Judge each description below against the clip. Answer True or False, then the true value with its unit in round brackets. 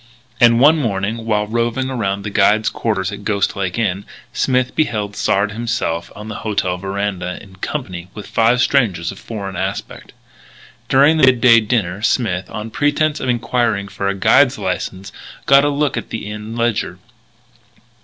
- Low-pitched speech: True (110 Hz)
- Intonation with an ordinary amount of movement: True (3.6 semitones)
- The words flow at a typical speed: True (165 wpm)